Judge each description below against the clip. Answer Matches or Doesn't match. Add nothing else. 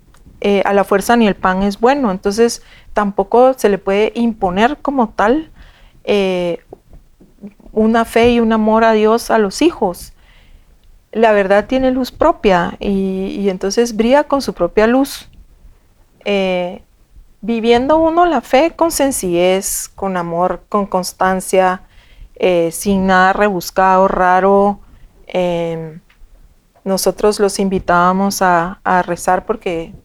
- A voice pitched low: Doesn't match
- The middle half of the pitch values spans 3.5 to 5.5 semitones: Matches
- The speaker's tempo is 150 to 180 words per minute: Doesn't match